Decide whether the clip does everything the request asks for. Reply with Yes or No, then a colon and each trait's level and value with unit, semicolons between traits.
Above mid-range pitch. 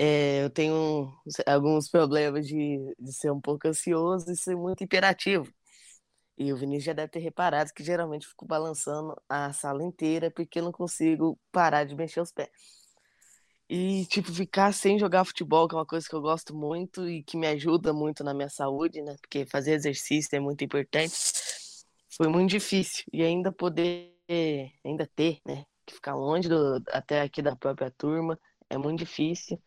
No: medium, 160 Hz